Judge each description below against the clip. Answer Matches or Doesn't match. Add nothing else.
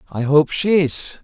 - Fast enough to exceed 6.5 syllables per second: Doesn't match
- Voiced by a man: Matches